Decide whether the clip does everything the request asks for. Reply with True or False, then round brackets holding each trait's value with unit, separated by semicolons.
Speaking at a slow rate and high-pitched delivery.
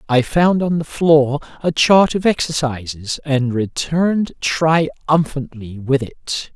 False (130 wpm; 145 Hz)